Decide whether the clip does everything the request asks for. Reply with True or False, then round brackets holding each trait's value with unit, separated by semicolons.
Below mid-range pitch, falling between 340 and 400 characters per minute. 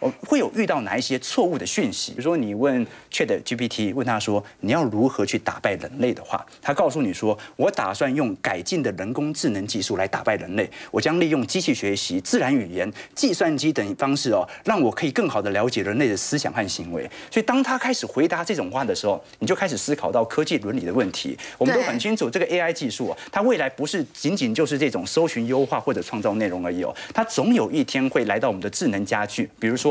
False (150 Hz; 360 characters per minute)